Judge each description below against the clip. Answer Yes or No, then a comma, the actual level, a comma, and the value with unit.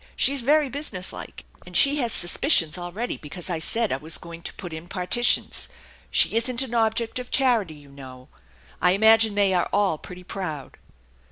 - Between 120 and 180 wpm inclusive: Yes, average, 175 wpm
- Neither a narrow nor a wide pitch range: No, wide, 5.7 semitones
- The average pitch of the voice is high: Yes, high, 195 Hz